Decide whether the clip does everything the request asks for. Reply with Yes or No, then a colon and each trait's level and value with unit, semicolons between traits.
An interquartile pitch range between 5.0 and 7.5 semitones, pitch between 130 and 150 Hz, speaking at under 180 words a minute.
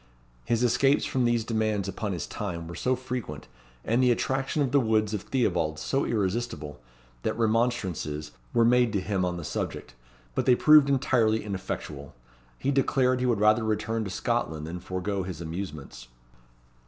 No: wide, 5.6 semitones; low, 110 Hz; average, 165 wpm